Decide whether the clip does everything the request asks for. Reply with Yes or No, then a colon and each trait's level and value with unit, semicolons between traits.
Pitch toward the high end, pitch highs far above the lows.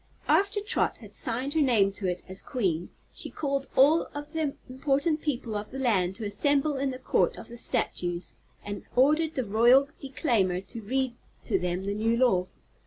Yes: very high, 255 Hz; wide, 5.7 semitones